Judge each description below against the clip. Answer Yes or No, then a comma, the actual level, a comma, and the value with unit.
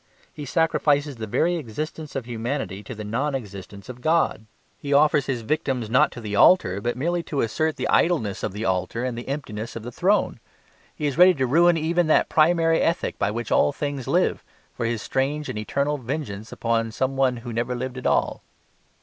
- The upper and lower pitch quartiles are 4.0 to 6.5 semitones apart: Yes, average, 4.9 semitones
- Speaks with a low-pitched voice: Yes, low, 130 Hz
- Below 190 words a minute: No, average, 200 wpm